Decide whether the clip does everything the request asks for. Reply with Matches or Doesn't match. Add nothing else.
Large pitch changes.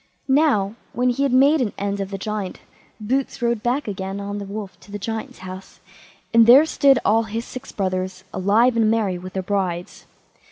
Doesn't match